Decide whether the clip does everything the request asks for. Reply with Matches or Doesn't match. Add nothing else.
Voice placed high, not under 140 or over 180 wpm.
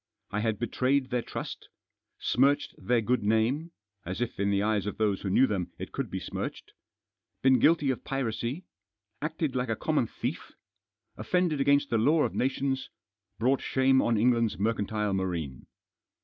Doesn't match